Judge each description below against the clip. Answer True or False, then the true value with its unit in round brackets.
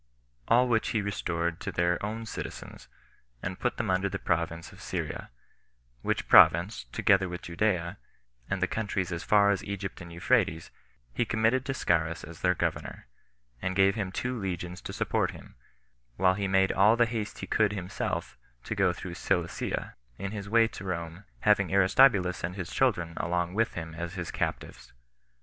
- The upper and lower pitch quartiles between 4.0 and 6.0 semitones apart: False (3.5 semitones)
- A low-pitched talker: True (95 Hz)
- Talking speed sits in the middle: True (175 wpm)